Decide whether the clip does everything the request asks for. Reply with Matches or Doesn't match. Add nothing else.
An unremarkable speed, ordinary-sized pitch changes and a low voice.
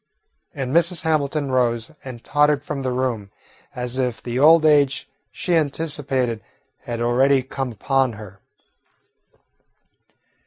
Doesn't match